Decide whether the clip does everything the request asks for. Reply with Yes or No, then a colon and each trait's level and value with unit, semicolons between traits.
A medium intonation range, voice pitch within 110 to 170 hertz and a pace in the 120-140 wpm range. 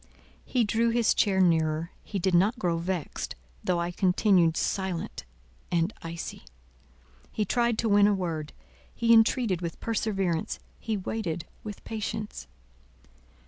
No: average, 4.3 semitones; high, 190 Hz; slow, 135 wpm